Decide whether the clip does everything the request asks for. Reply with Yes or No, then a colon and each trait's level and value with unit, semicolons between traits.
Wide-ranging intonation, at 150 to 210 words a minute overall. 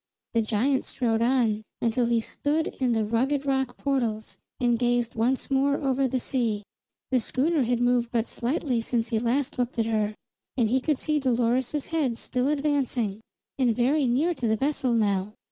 No: average, 2.9 semitones; average, 175 wpm